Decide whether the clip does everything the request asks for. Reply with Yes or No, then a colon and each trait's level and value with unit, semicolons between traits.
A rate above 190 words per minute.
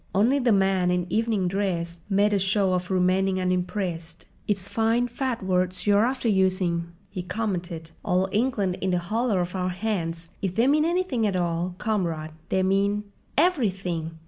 No: average, 165 wpm